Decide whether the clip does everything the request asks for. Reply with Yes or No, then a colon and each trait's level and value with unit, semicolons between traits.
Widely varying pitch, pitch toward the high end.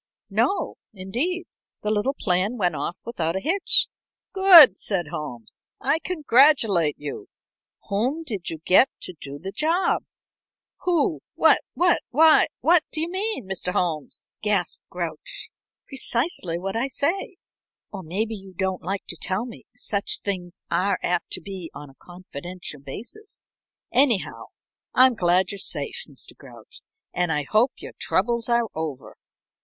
Yes: wide, 7.7 semitones; high, 200 Hz